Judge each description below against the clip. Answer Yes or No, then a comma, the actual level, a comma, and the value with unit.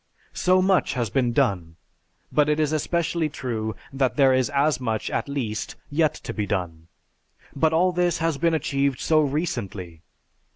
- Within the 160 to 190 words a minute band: Yes, average, 165 wpm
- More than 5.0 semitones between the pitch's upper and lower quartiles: Yes, wide, 5.6 semitones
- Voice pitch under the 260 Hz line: Yes, medium, 140 Hz